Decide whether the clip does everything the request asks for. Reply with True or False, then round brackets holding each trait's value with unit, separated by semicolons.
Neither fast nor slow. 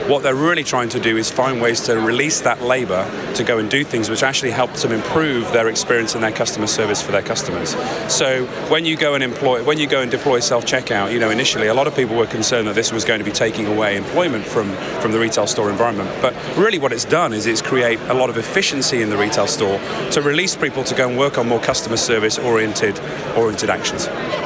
False (240 wpm)